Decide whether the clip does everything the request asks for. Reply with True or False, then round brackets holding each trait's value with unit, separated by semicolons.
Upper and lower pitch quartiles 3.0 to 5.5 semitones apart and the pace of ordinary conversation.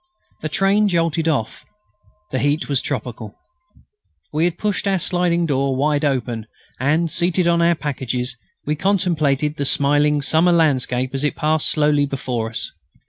True (3.8 semitones; 150 wpm)